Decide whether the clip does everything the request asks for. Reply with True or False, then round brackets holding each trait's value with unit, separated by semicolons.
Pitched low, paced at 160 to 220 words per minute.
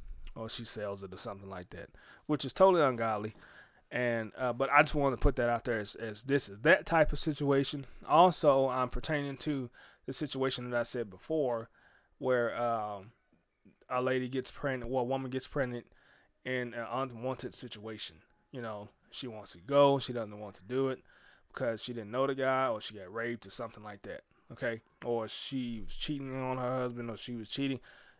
True (125 Hz; 200 wpm)